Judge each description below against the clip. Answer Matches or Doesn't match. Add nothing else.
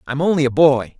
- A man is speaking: Matches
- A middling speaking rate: Doesn't match